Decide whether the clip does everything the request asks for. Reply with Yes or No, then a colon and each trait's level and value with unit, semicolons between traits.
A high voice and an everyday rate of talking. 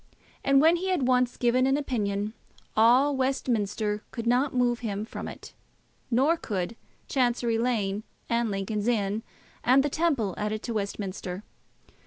Yes: high, 235 Hz; average, 145 wpm